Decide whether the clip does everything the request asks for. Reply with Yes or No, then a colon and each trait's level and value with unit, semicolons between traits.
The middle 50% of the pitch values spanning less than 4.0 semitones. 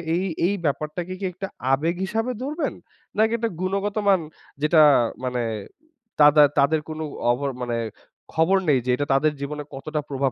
No: wide, 5.5 semitones